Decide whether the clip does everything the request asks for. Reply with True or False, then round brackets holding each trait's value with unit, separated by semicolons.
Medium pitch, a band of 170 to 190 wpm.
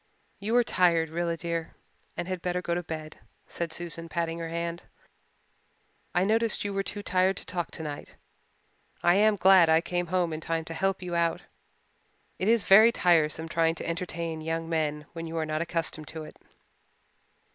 True (170 Hz; 180 wpm)